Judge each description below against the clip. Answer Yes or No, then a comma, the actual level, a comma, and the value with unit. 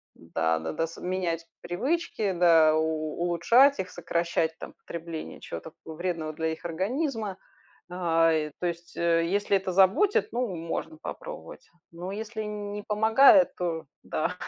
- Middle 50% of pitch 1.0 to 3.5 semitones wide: No, average, 4.4 semitones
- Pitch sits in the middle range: Yes, medium, 175 Hz